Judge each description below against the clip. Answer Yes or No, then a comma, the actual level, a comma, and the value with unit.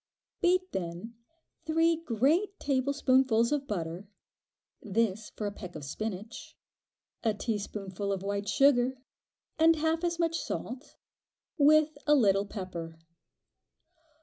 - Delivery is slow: Yes, slow, 115 wpm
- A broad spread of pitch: Yes, wide, 7.2 semitones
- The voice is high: Yes, high, 230 Hz